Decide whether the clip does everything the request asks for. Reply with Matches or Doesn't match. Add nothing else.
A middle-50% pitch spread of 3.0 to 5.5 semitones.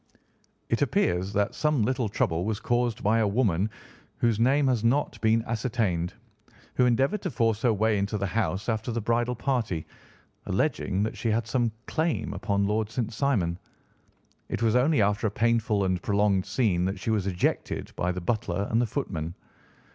Matches